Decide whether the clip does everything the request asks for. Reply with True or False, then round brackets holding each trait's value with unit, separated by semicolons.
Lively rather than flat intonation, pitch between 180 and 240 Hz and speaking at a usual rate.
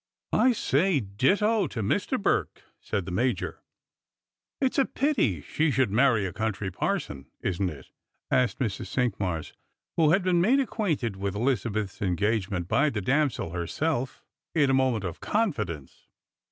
False (8.0 semitones; 120 Hz; 155 wpm)